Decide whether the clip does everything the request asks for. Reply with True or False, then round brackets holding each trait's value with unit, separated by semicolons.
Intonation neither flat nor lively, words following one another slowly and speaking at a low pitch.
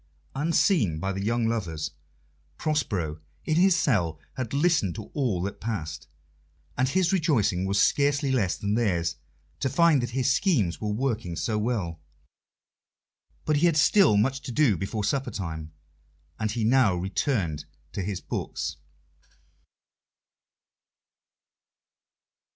False (6.8 semitones; 130 wpm; 110 Hz)